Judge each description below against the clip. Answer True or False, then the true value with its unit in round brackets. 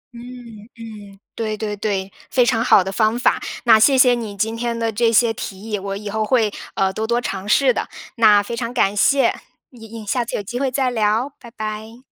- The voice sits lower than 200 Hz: False (225 Hz)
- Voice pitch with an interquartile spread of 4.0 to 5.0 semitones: False (2.5 semitones)